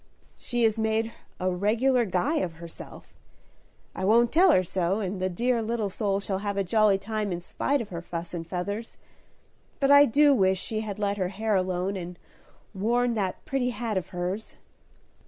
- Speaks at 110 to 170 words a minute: No, average, 185 wpm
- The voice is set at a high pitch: Yes, high, 205 Hz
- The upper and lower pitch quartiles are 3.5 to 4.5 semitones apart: Yes, average, 3.8 semitones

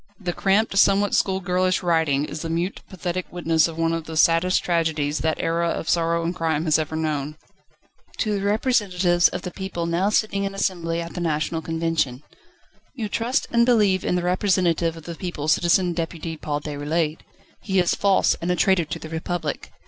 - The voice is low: No, medium, 170 Hz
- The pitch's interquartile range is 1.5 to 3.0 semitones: Yes, average, 2.7 semitones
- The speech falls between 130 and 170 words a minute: No, average, 190 wpm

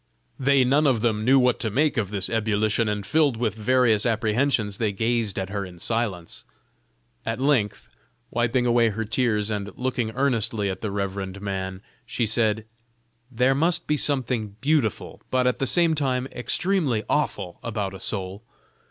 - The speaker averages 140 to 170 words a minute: Yes, average, 165 wpm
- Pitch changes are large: No, average, 3.8 semitones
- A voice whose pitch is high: No, low, 115 Hz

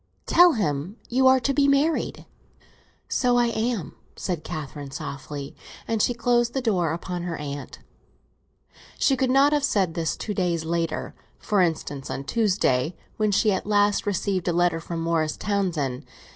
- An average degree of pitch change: No, wide, 6.6 semitones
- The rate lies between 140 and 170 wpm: Yes, average, 160 wpm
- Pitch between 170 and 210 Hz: Yes, high, 190 Hz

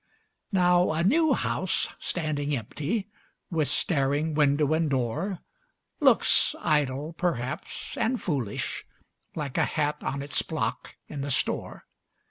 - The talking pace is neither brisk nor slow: No, slow, 120 wpm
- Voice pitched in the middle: Yes, medium, 150 Hz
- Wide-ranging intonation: No, average, 3.8 semitones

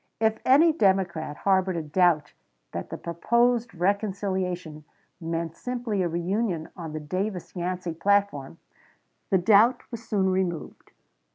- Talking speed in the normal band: No, slow, 125 wpm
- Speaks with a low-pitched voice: No, medium, 185 Hz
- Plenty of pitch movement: No, average, 3.7 semitones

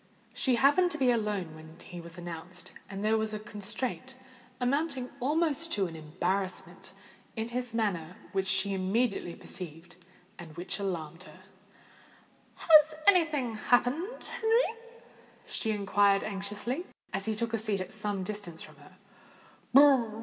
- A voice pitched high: Yes, high, 210 Hz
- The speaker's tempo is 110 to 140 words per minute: Yes, slow, 135 wpm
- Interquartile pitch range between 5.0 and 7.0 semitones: Yes, wide, 5.4 semitones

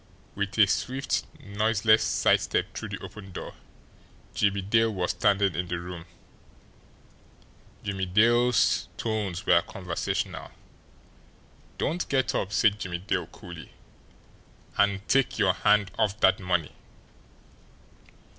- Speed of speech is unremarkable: No, slow, 115 wpm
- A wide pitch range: No, average, 3.2 semitones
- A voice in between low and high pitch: No, low, 100 Hz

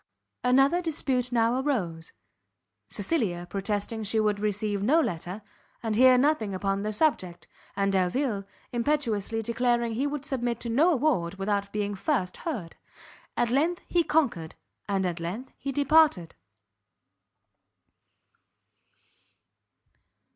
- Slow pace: Yes, slow, 120 wpm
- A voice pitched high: Yes, high, 225 Hz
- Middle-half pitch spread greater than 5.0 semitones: Yes, wide, 5.6 semitones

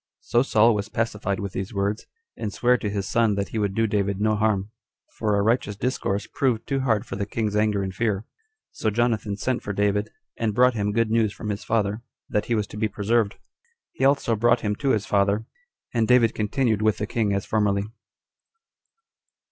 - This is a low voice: Yes, low, 105 Hz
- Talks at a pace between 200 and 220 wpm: Yes, fast, 205 wpm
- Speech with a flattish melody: Yes, narrow, 2.2 semitones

